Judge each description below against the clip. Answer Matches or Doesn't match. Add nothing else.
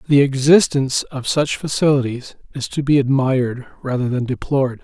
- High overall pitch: Doesn't match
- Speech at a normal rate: Matches